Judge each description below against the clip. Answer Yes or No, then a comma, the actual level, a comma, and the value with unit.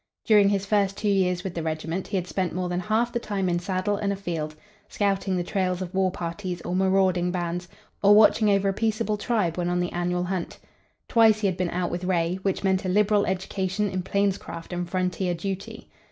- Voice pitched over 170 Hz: Yes, medium, 185 Hz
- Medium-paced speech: No, fast, 210 wpm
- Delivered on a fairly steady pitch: Yes, narrow, 2.1 semitones